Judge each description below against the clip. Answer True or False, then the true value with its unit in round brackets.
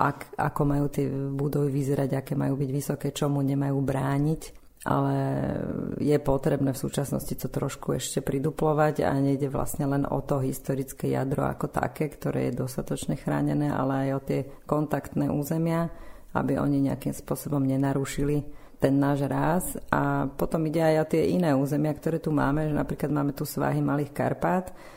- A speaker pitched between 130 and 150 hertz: True (140 Hz)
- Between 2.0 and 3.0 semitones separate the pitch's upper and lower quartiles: False (1.4 semitones)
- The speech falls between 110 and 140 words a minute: False (165 wpm)